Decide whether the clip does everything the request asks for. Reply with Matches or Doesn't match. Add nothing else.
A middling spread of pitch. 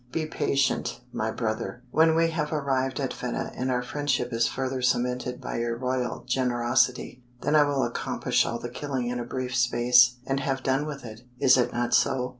Doesn't match